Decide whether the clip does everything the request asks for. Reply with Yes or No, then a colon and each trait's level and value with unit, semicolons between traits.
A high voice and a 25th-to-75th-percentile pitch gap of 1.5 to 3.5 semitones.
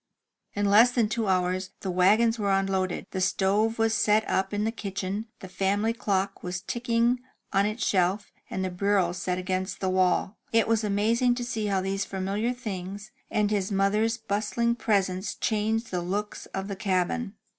Yes: high, 200 Hz; average, 2.9 semitones